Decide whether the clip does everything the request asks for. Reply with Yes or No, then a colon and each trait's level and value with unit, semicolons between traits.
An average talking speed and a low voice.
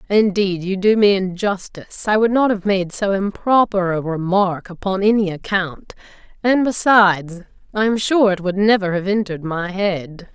No: average, 170 wpm; high, 195 Hz